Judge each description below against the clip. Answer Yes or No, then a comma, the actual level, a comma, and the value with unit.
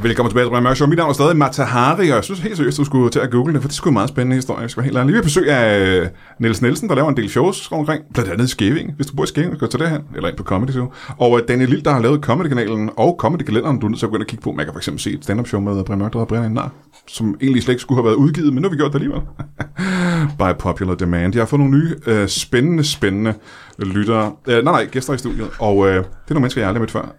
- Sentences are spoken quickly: Yes, fast, 300 wpm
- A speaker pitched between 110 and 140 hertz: Yes, low, 125 Hz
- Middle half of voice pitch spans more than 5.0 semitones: No, average, 4.7 semitones